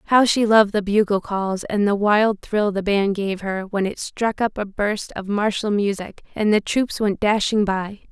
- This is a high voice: Yes, high, 205 Hz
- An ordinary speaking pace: No, fast, 215 wpm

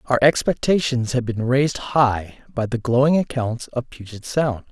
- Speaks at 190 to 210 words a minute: No, average, 165 wpm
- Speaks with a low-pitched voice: Yes, low, 125 Hz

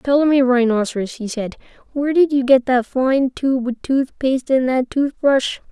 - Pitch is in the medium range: No, very high, 260 Hz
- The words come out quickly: No, average, 190 wpm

